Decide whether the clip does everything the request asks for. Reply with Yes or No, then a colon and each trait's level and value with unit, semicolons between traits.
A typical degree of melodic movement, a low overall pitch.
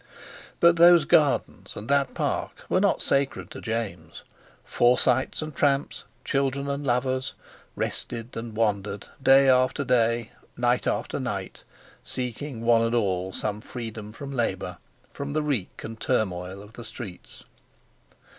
Yes: average, 3.9 semitones; low, 120 Hz